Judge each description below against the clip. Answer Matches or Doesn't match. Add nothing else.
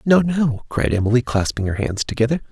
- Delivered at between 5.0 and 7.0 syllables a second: Matches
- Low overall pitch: Matches